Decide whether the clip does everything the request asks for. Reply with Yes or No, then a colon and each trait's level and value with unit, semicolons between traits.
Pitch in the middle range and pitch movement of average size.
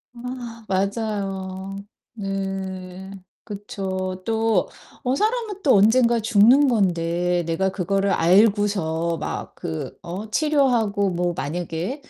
No: high, 195 Hz; average, 3.5 semitones